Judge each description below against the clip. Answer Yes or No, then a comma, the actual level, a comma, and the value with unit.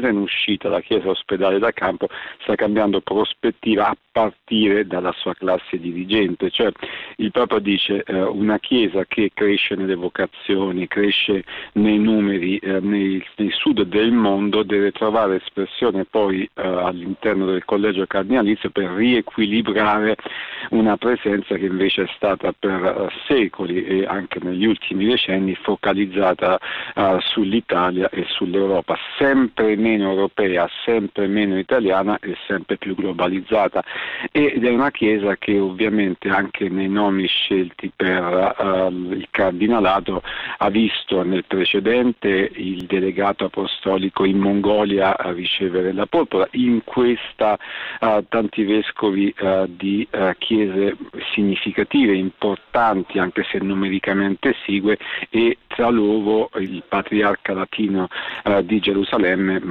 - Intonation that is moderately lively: No, narrow, 1.9 semitones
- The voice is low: Yes, low, 100 Hz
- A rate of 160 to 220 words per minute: No, average, 125 wpm